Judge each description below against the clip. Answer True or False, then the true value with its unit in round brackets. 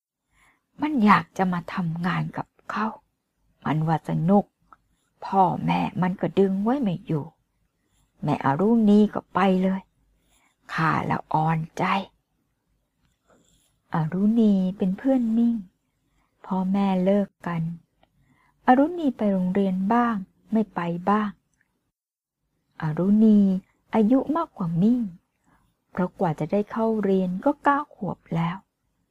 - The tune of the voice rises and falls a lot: False (4.1 semitones)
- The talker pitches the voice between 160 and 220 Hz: True (190 Hz)